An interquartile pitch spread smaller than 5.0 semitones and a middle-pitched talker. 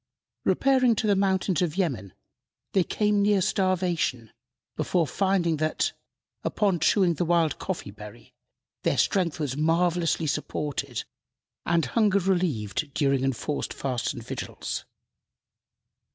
No: average, 5.3 semitones; medium, 170 Hz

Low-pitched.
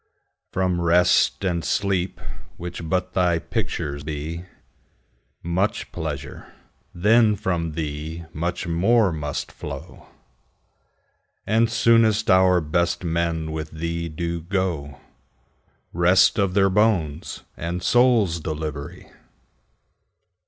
Yes: very low, 85 Hz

